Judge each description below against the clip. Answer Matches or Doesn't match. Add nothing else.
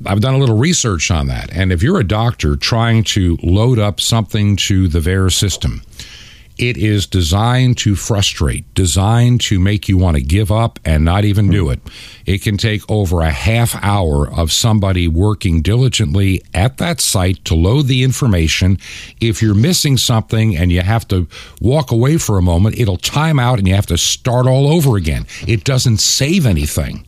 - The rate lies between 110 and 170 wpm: Doesn't match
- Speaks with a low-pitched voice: Matches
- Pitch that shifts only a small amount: Doesn't match